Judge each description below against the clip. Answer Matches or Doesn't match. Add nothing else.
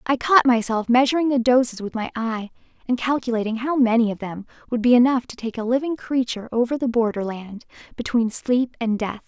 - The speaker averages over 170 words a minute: Matches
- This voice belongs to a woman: Matches